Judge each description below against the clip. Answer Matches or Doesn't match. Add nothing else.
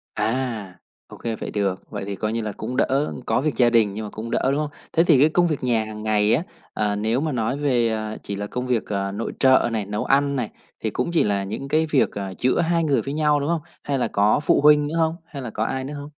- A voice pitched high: Doesn't match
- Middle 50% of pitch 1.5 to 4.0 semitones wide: Doesn't match